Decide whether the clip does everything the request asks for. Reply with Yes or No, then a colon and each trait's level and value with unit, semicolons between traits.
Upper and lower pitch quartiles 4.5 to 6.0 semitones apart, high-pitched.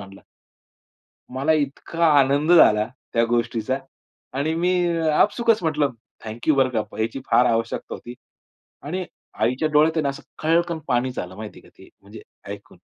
No: average, 5.3 semitones; low, 135 Hz